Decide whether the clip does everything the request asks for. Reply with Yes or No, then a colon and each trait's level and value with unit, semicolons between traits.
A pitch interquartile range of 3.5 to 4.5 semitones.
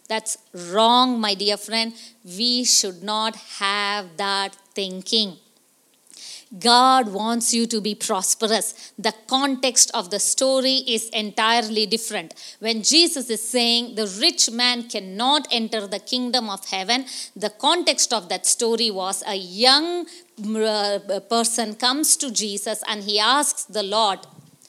No: average, 3.1 semitones